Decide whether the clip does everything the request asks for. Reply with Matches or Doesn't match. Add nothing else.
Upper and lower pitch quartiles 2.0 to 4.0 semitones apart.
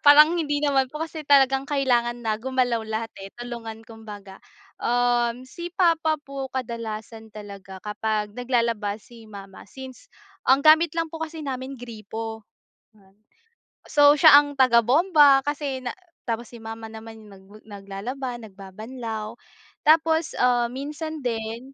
Doesn't match